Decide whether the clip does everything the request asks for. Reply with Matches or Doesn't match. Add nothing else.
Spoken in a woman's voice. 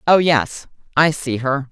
Matches